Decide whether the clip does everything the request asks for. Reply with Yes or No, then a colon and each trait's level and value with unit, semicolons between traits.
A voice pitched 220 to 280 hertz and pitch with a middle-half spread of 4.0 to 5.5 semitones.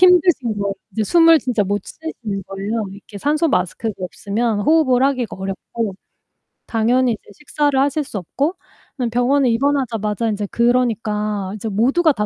Yes: high, 235 Hz; average, 5.1 semitones